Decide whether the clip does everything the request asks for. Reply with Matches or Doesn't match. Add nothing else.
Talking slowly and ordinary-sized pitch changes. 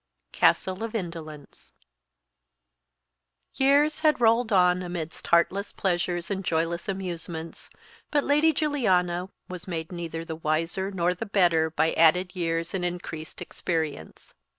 Matches